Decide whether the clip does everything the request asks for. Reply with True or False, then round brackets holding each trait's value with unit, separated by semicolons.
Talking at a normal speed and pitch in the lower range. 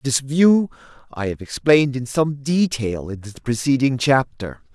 True (150 wpm; 130 Hz)